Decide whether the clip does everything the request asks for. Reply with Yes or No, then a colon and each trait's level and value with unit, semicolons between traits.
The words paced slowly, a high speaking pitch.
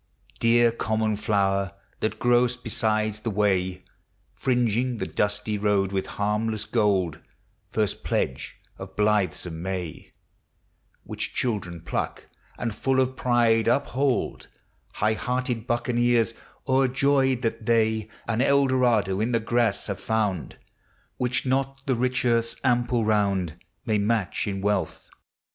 No: slow, 125 wpm; low, 110 Hz